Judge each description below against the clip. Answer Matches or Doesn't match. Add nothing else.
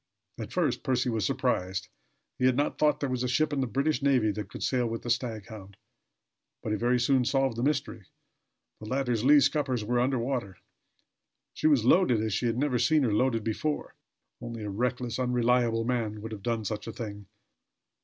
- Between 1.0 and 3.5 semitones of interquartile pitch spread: Matches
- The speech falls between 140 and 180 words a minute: Doesn't match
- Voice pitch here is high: Doesn't match